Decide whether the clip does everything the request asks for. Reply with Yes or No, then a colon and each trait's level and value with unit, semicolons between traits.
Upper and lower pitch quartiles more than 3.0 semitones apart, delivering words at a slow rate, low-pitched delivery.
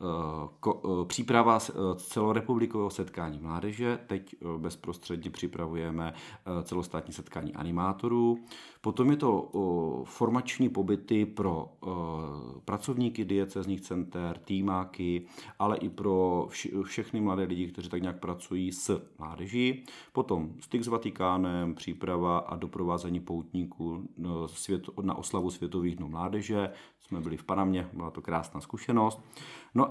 Yes: average, 3.6 semitones; slow, 110 wpm; very low, 90 Hz